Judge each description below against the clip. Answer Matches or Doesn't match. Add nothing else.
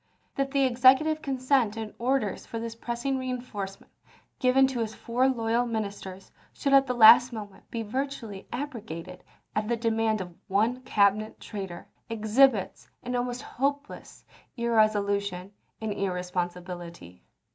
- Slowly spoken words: Matches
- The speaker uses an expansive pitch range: Doesn't match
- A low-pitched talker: Doesn't match